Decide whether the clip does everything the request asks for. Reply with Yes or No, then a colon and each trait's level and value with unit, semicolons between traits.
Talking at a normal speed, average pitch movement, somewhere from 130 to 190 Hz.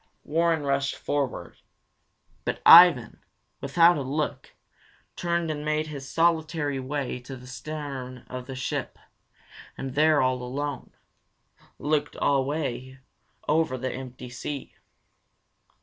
No: slow, 115 wpm; average, 3.1 semitones; medium, 140 Hz